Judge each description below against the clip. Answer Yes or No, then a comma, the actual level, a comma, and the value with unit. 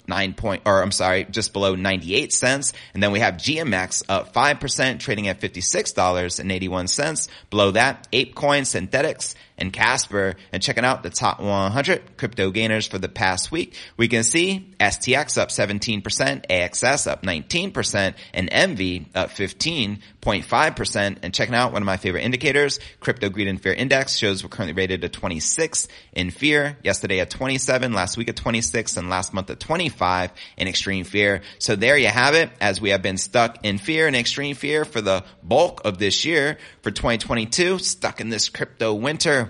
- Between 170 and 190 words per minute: Yes, average, 175 wpm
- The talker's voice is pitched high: No, low, 105 Hz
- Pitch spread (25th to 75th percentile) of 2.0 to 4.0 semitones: No, wide, 5.5 semitones